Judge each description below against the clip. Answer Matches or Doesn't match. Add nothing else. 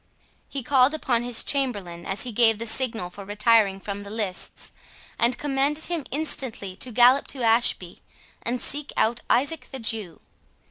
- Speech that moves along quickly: Doesn't match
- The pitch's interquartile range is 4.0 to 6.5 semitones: Matches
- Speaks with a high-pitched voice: Matches